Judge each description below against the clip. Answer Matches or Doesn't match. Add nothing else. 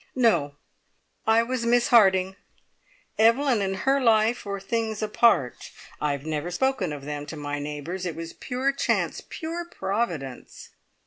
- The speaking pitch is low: Doesn't match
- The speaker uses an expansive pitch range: Matches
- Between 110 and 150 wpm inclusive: Matches